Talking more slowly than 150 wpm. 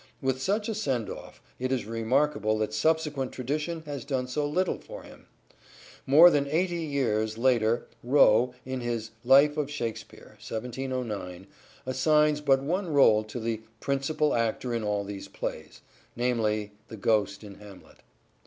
No: average, 155 wpm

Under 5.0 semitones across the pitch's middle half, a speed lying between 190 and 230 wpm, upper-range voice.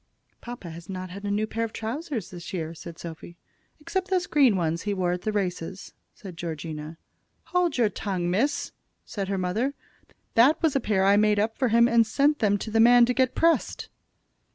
No: wide, 5.5 semitones; average, 200 wpm; high, 210 Hz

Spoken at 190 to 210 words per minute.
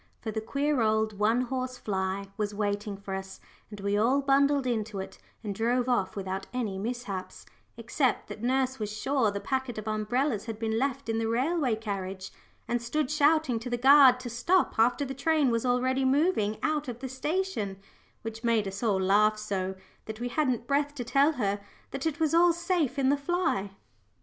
Yes: average, 195 wpm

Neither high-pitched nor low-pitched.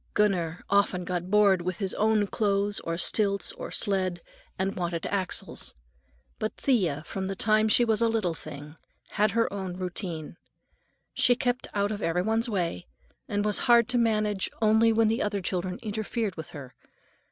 No: high, 200 Hz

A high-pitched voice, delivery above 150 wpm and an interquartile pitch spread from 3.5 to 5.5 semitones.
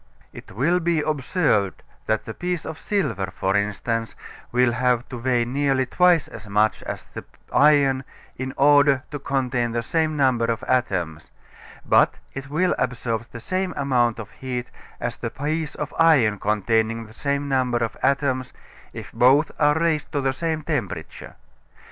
No: low, 130 Hz; average, 160 wpm; average, 4.2 semitones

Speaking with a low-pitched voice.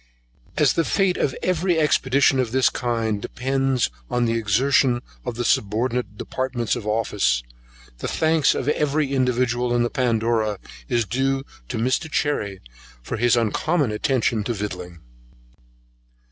Yes: low, 120 Hz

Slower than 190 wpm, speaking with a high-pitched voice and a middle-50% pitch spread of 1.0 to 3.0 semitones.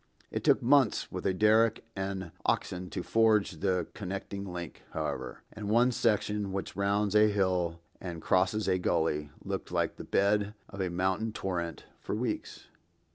No: average, 160 wpm; low, 100 Hz; narrow, 2.6 semitones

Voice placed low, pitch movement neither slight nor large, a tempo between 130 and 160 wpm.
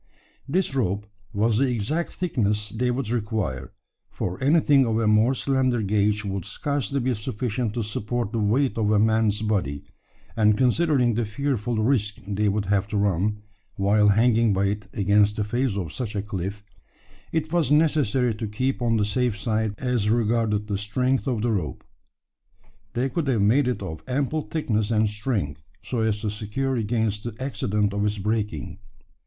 No: low, 110 Hz; average, 3.4 semitones; average, 175 wpm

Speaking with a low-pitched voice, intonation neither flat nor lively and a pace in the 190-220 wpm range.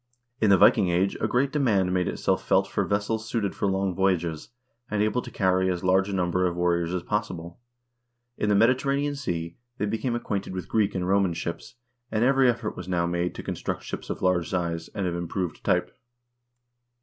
Yes: very low, 95 Hz; average, 3.5 semitones; average, 195 wpm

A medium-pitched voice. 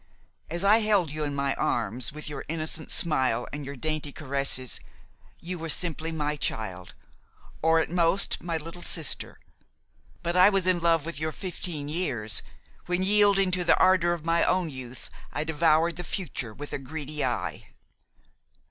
Yes: medium, 160 Hz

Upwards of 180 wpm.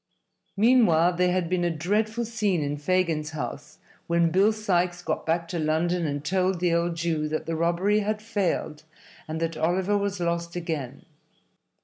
No: average, 165 wpm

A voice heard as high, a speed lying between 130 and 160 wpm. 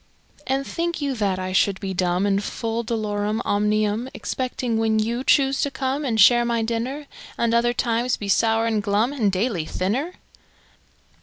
No: high, 225 Hz; average, 170 wpm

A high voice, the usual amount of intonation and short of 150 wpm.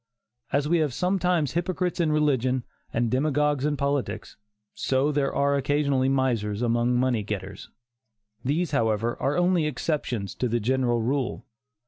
No: low, 135 Hz; average, 3.9 semitones; average, 140 wpm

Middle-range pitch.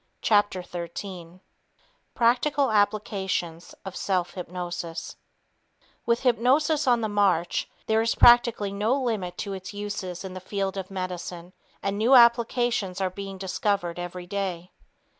No: high, 195 Hz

